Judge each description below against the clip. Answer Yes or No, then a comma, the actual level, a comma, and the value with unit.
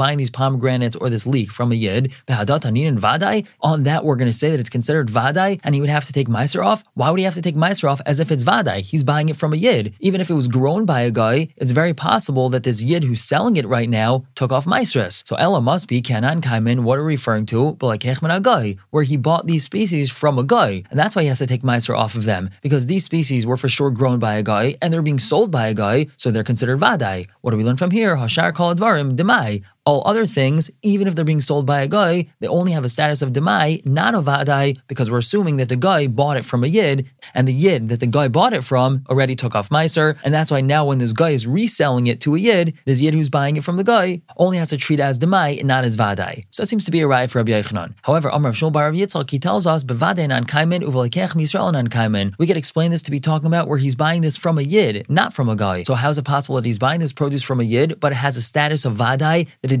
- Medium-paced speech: No, fast, 265 wpm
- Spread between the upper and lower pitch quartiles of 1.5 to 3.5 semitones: No, average, 4.3 semitones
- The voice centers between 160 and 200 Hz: No, medium, 140 Hz